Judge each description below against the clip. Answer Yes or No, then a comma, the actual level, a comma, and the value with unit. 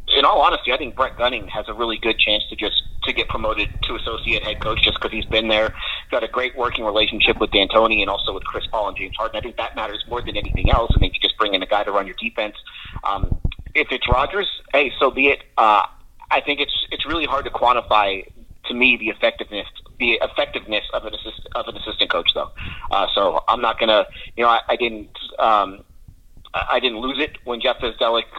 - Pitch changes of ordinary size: No, narrow, 2.2 semitones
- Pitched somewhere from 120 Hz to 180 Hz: No, low, 110 Hz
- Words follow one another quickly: Yes, fast, 235 wpm